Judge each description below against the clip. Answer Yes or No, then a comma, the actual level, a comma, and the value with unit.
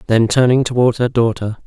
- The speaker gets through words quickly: No, average, 180 wpm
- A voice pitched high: No, low, 120 Hz